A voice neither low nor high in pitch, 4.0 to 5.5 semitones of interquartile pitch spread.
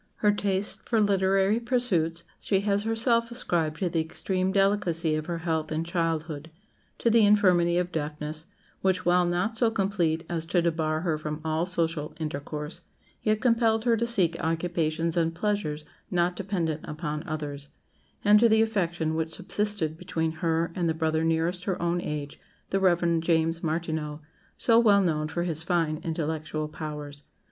No: medium, 170 Hz; average, 3.6 semitones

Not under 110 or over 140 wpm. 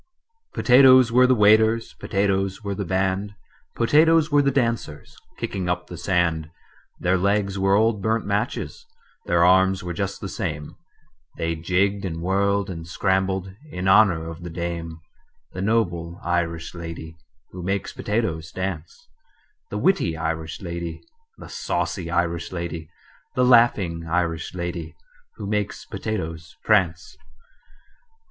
Yes: slow, 135 wpm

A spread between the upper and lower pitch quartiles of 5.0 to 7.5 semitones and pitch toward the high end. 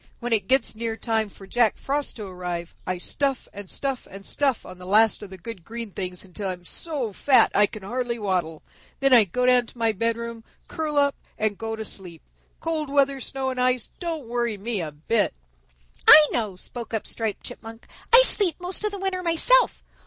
Yes: average, 5.3 semitones; high, 230 Hz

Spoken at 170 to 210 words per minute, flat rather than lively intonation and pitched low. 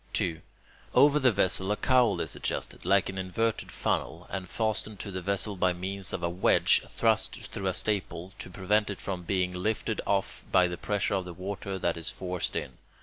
Yes: average, 200 wpm; narrow, 2.2 semitones; very low, 95 Hz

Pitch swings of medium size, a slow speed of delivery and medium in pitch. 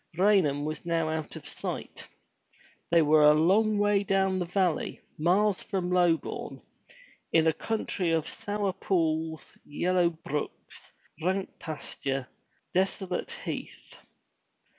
Yes: average, 3.4 semitones; slow, 120 wpm; medium, 175 Hz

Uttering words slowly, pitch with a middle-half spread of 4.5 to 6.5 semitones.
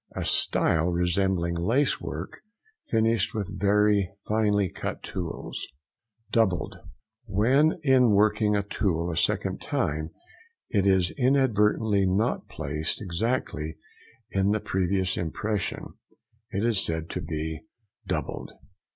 No: slow, 110 wpm; average, 3.8 semitones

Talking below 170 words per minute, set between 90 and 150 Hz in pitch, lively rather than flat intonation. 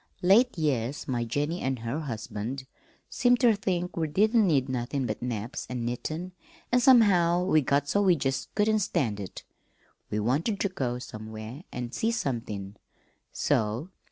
Yes: average, 155 wpm; medium, 140 Hz; wide, 7.6 semitones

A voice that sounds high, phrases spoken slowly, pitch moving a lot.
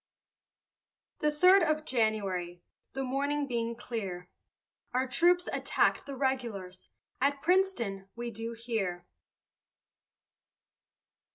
Yes: high, 240 Hz; slow, 95 wpm; wide, 6.2 semitones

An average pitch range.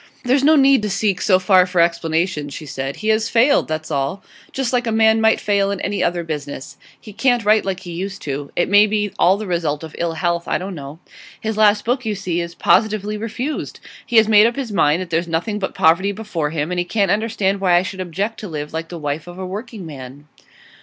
Yes: average, 4.7 semitones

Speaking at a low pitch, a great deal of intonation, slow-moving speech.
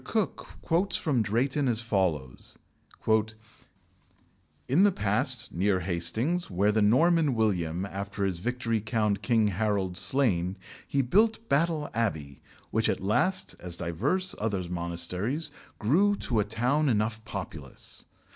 Yes: low, 110 Hz; wide, 6.8 semitones; slow, 130 wpm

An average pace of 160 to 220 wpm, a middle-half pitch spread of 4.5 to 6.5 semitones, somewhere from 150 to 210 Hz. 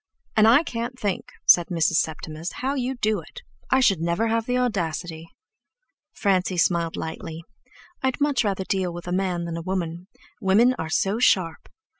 Yes: average, 170 wpm; average, 5.3 semitones; high, 190 Hz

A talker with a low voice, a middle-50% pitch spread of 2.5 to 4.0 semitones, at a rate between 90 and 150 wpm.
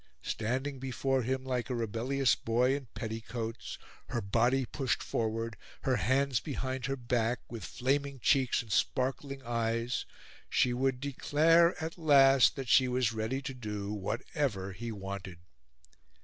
Yes: low, 125 Hz; average, 2.9 semitones; average, 140 wpm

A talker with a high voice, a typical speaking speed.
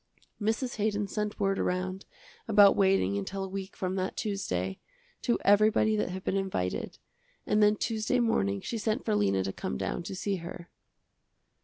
Yes: high, 195 Hz; average, 170 wpm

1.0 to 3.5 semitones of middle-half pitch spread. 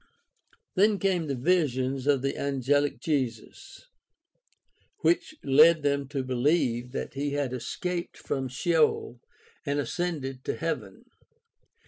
No: average, 4.1 semitones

